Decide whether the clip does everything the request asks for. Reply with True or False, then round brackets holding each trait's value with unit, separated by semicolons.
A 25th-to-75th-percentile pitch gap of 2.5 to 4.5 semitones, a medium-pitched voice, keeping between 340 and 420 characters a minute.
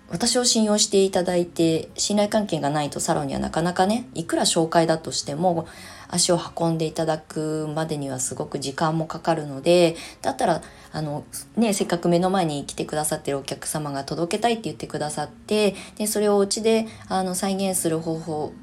True (4.0 semitones; 165 Hz; 385 characters per minute)